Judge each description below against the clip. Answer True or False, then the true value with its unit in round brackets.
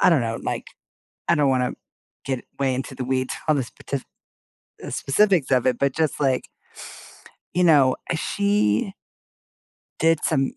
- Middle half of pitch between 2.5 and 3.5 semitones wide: False (3.9 semitones)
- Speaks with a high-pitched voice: False (135 Hz)